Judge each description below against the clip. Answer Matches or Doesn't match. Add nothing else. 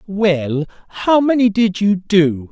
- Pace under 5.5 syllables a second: Matches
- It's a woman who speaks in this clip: Doesn't match